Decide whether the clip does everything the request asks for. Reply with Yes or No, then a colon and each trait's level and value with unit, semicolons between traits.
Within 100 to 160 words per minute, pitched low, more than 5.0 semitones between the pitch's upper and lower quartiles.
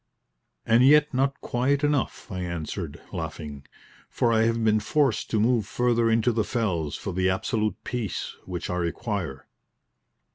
Yes: average, 150 wpm; low, 110 Hz; wide, 5.4 semitones